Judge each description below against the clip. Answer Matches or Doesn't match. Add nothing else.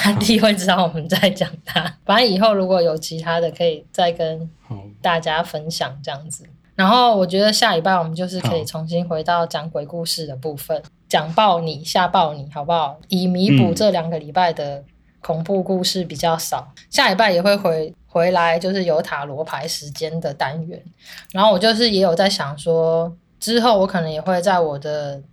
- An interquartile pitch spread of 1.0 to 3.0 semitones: Matches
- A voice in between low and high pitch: Matches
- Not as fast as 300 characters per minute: Matches